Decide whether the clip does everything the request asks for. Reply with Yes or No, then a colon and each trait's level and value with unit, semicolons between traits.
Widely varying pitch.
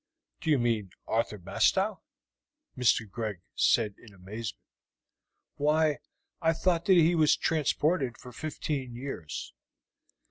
Yes: wide, 5.9 semitones